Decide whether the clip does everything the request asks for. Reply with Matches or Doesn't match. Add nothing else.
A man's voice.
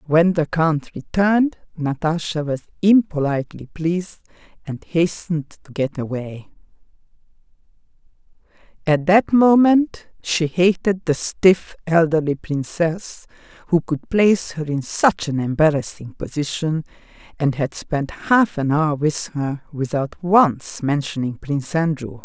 Doesn't match